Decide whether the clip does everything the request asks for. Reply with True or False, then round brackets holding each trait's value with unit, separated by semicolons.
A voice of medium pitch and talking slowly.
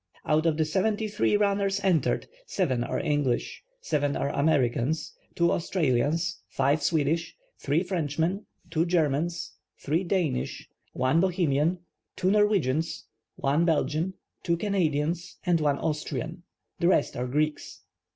True (160 Hz; 125 wpm)